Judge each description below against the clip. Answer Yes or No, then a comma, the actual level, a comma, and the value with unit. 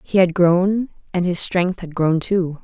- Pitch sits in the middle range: Yes, medium, 180 Hz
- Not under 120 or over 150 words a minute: No, fast, 205 wpm